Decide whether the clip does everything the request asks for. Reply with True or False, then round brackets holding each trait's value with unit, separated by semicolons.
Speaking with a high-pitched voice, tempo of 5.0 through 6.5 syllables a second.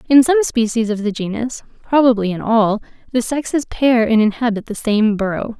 True (230 Hz; 5.3 syllables/s)